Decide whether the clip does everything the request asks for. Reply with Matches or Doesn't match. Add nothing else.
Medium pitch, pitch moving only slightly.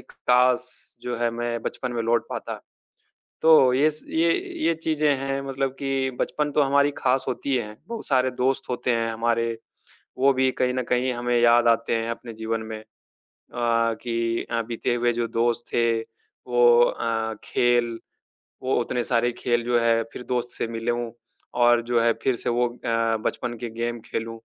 Doesn't match